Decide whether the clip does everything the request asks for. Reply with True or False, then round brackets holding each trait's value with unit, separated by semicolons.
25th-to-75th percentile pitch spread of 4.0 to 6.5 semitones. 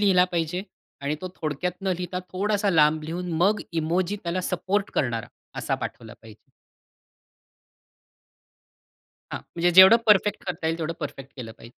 False (3.4 semitones)